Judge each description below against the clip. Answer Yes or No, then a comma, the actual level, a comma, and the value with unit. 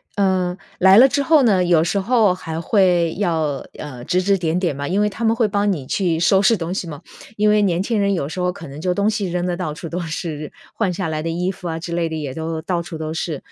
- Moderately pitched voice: Yes, medium, 180 Hz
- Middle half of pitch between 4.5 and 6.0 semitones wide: No, average, 3.5 semitones